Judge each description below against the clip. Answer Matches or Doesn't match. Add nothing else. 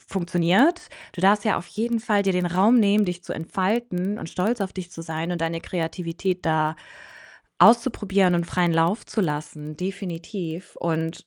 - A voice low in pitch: Doesn't match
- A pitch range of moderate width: Matches